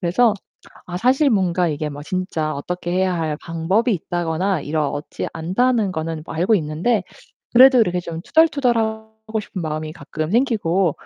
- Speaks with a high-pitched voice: No, medium, 180 Hz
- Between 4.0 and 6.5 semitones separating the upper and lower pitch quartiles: Yes, average, 5.3 semitones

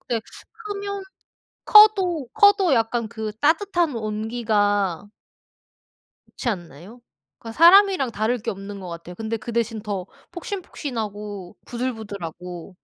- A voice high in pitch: Yes, high, 225 Hz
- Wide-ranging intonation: Yes, wide, 8.2 semitones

